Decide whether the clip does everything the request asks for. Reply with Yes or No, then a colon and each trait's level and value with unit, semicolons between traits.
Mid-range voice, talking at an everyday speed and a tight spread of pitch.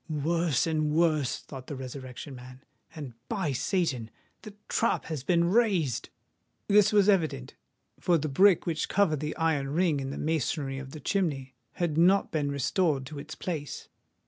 No: medium, 155 Hz; average, 165 wpm; average, 4.1 semitones